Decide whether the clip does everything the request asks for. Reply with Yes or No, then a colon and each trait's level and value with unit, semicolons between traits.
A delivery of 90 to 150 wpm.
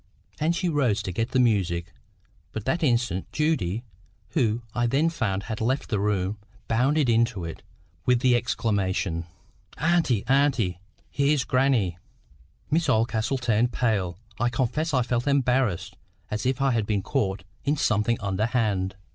Yes: average, 145 wpm